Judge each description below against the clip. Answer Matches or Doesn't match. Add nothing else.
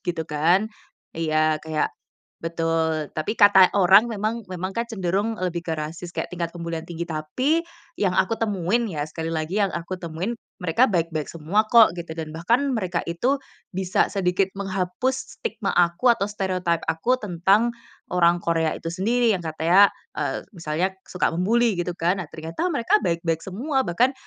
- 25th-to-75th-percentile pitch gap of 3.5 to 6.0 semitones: Matches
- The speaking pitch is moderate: Matches